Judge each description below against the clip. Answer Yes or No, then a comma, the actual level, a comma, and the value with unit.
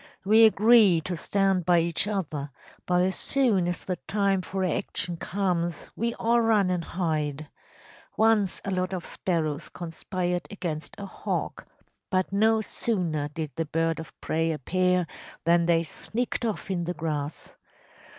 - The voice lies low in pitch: No, medium, 180 Hz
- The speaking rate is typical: Yes, average, 150 wpm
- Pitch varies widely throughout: No, average, 3.4 semitones